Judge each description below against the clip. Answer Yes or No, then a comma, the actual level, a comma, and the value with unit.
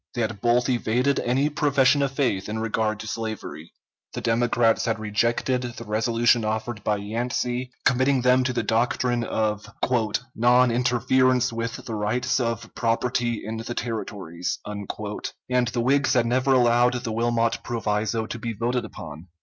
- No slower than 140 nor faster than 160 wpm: Yes, average, 155 wpm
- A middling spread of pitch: No, narrow, 2.2 semitones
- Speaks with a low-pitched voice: Yes, low, 120 Hz